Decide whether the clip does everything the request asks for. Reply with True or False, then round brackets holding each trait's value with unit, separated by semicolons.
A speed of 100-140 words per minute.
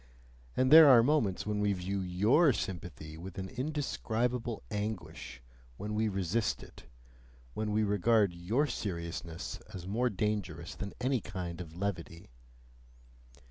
True (135 wpm)